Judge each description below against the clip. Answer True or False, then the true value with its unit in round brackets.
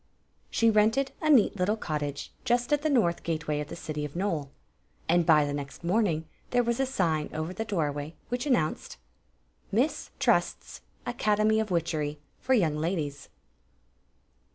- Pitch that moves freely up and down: True (6.9 semitones)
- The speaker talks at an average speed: True (165 wpm)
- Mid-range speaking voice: True (175 Hz)